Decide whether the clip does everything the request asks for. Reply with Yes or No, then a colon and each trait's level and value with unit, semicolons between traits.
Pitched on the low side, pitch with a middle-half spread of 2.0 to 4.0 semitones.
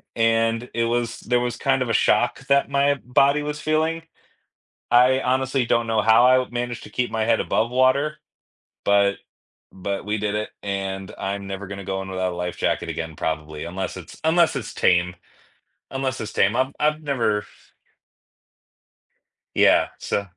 No: low, 115 Hz; average, 4.8 semitones